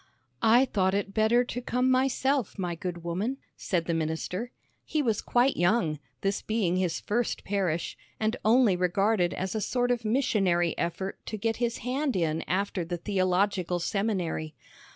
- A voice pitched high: Yes, high, 200 Hz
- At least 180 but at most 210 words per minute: No, average, 160 wpm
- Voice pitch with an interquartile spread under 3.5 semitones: No, average, 5.0 semitones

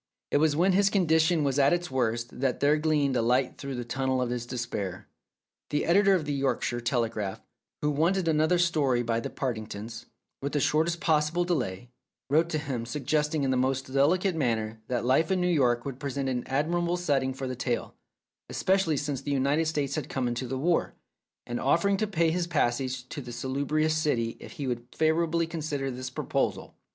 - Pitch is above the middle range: No, medium, 140 Hz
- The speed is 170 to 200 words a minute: Yes, average, 195 wpm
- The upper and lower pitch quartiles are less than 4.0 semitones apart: No, average, 4.3 semitones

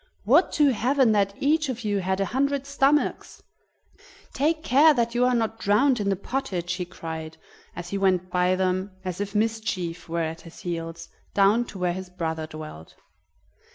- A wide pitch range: Yes, wide, 5.8 semitones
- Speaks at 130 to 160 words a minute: No, average, 180 wpm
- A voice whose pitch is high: Yes, high, 200 Hz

